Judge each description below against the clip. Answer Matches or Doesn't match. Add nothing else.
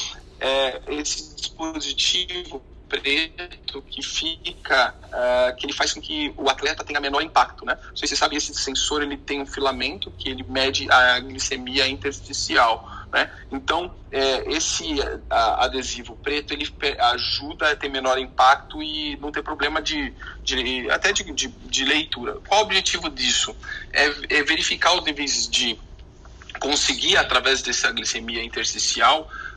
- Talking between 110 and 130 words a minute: Doesn't match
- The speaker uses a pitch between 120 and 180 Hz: Matches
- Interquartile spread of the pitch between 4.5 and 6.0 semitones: Doesn't match